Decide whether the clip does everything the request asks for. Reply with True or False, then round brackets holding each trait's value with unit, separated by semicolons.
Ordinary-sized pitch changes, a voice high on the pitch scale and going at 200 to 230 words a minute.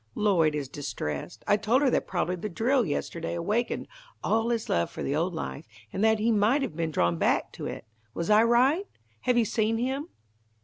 False (6.2 semitones; 210 Hz; 205 wpm)